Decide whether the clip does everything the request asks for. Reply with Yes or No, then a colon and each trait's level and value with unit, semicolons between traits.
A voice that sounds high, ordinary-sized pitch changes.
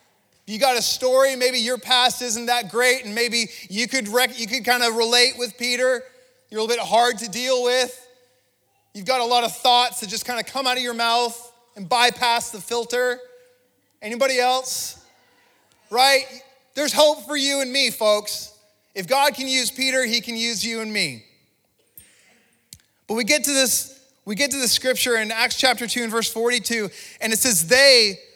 No: high, 245 Hz; narrow, 1.8 semitones